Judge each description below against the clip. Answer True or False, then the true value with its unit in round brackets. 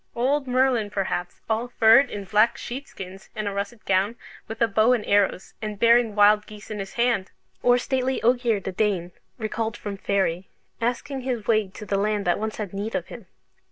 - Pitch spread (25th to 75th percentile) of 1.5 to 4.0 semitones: True (3.1 semitones)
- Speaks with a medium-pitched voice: False (215 Hz)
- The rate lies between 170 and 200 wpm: True (195 wpm)